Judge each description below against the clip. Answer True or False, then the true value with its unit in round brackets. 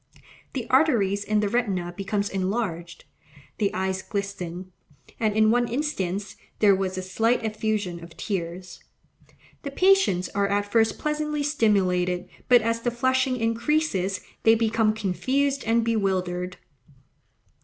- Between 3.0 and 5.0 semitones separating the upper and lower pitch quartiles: True (4.1 semitones)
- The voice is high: True (210 Hz)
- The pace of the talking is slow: True (130 wpm)